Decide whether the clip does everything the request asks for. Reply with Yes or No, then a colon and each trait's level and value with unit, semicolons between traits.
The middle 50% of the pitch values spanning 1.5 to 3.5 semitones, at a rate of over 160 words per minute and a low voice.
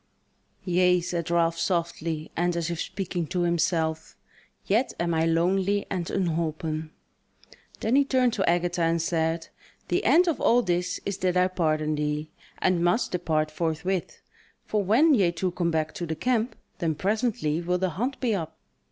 No: average, 2.8 semitones; average, 170 wpm; medium, 175 Hz